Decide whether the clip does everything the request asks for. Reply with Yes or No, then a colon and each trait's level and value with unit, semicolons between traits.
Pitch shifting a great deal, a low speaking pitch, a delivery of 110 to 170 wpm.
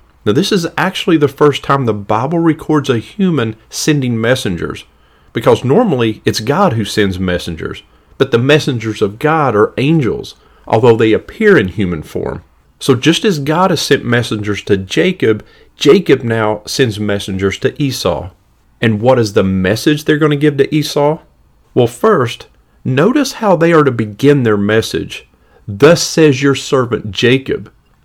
Yes: wide, 6.0 semitones; low, 130 Hz; average, 160 wpm